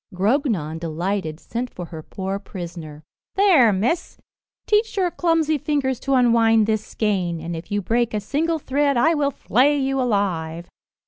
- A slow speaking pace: No, average, 155 wpm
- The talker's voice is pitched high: Yes, high, 225 Hz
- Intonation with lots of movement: Yes, wide, 7.9 semitones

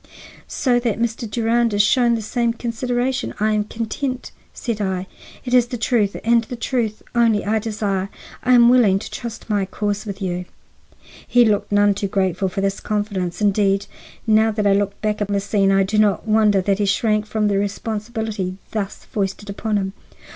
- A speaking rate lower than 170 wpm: No, average, 190 wpm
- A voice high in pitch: Yes, high, 210 Hz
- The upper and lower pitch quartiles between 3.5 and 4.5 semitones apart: No, narrow, 2.5 semitones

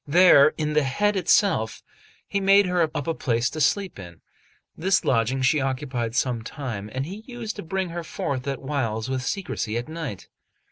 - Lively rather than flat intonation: Yes, wide, 6.3 semitones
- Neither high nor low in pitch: Yes, medium, 145 Hz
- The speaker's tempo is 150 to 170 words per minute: No, average, 185 wpm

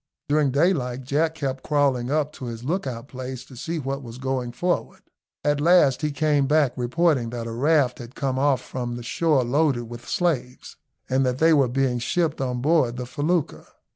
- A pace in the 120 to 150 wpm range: No, average, 190 wpm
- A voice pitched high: No, low, 135 Hz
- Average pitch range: Yes, average, 3.5 semitones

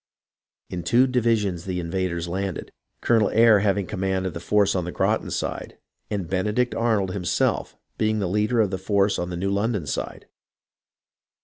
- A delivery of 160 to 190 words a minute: Yes, average, 175 wpm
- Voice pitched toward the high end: No, low, 100 Hz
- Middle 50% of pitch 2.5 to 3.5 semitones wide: Yes, average, 2.8 semitones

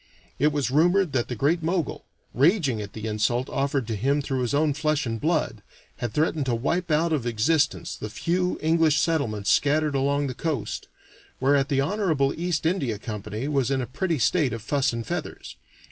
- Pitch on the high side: No, medium, 140 Hz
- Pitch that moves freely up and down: No, average, 4.7 semitones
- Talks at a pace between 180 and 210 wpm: Yes, average, 190 wpm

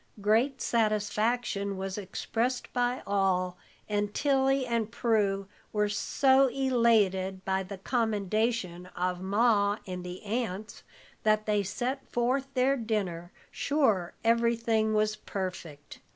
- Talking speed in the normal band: No, slow, 115 wpm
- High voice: Yes, high, 215 Hz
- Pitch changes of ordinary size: Yes, average, 3.7 semitones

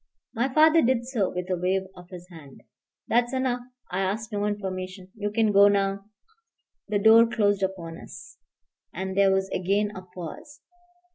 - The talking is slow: No, average, 165 wpm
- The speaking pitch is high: Yes, high, 200 Hz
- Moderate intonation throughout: Yes, average, 3.5 semitones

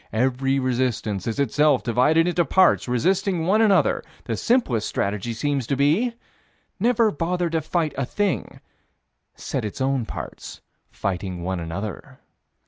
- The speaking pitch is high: No, low, 135 Hz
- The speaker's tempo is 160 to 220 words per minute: No, slow, 135 wpm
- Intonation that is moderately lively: No, wide, 7.5 semitones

